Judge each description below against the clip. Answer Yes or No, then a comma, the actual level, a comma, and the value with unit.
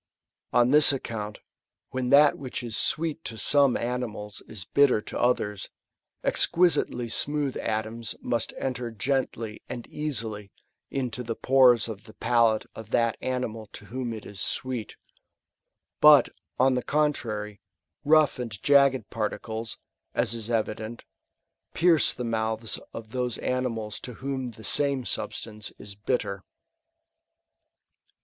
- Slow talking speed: Yes, slow, 130 wpm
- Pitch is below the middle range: Yes, low, 120 Hz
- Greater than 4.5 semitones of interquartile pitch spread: No, average, 3.2 semitones